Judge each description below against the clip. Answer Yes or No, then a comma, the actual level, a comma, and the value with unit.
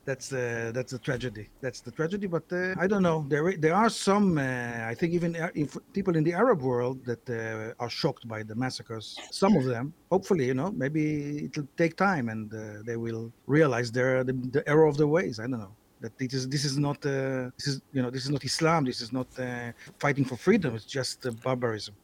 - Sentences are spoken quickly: Yes, fast, 225 wpm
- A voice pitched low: Yes, low, 130 Hz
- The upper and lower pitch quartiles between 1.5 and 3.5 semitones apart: No, average, 4.7 semitones